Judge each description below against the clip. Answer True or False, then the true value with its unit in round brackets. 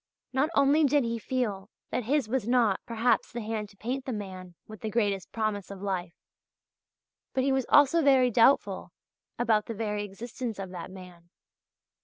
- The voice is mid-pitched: False (225 Hz)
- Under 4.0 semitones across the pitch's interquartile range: False (4.3 semitones)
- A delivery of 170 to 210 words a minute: True (175 wpm)